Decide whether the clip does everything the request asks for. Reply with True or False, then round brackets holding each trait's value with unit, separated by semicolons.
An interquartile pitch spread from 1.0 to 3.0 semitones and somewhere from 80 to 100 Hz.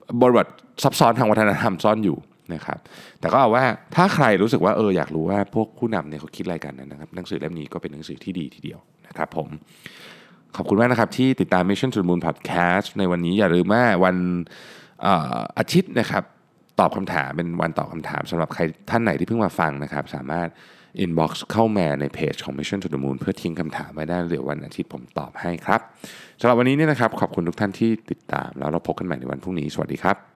False (5.5 semitones; 90 Hz)